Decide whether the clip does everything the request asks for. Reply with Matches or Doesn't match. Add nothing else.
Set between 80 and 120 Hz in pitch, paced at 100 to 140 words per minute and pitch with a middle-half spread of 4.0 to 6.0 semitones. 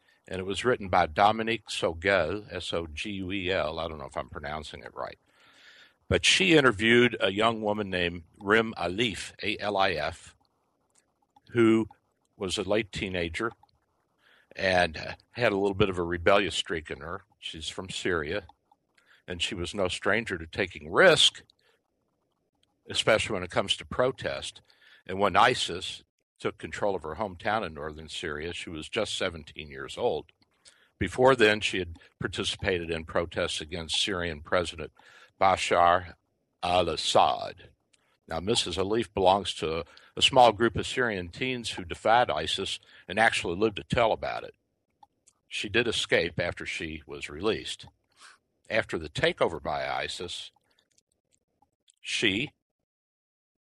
Matches